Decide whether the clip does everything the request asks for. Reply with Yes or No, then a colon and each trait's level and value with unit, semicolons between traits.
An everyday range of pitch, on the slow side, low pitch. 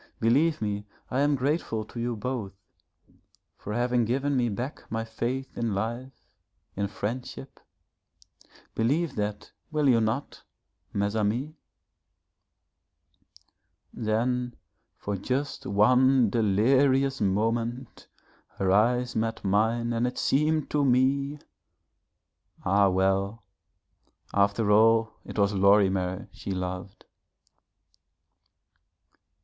Yes: average, 4.1 semitones; slow, 100 wpm; low, 115 Hz